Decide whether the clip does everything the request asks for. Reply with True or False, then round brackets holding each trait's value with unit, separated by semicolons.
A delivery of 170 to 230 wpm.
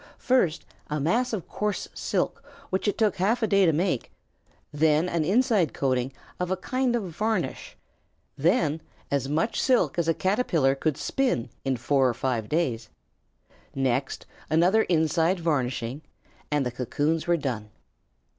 False (150 wpm)